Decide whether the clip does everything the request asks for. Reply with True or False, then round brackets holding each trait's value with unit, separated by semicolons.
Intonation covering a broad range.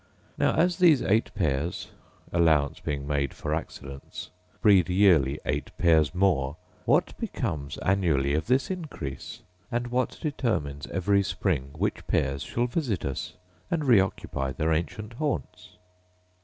True (8.7 semitones)